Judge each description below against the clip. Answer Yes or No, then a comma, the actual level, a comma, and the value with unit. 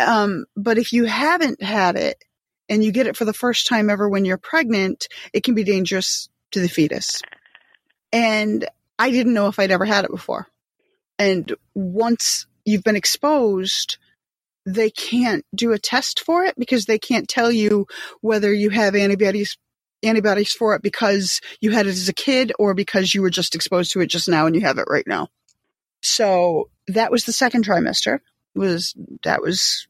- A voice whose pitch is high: Yes, high, 215 Hz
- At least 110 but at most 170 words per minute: No, average, 185 wpm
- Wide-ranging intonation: No, average, 3.2 semitones